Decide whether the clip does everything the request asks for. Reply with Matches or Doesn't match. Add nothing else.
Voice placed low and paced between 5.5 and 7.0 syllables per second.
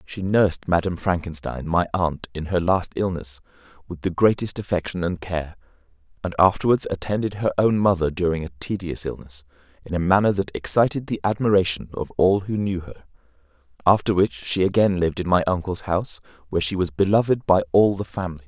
Matches